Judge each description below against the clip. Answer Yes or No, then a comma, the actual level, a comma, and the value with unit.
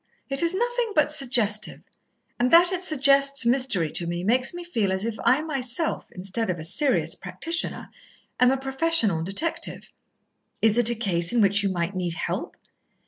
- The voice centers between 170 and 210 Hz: No, high, 245 Hz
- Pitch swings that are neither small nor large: No, wide, 7.5 semitones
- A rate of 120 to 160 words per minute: No, average, 175 wpm